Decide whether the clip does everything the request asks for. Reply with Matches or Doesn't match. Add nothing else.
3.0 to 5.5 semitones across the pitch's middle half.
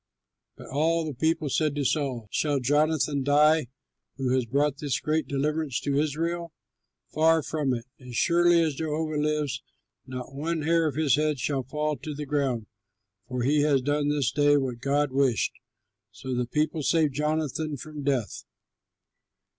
Doesn't match